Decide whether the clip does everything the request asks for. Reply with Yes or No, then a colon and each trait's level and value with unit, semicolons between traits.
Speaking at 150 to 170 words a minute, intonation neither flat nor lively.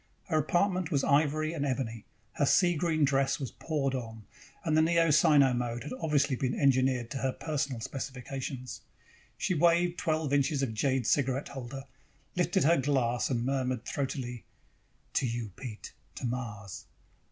Yes: average, 155 wpm; average, 3.7 semitones